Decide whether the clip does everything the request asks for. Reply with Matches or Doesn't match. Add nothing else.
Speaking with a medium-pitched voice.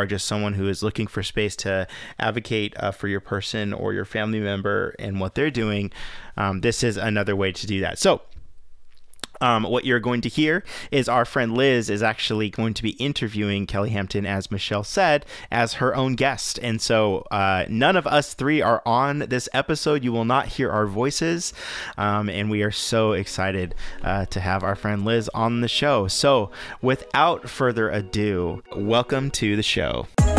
Doesn't match